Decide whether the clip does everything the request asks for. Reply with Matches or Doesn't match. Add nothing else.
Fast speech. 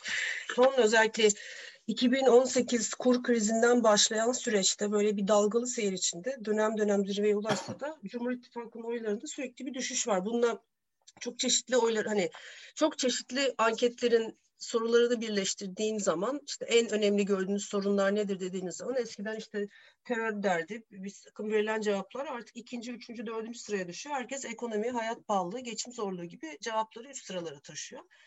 Matches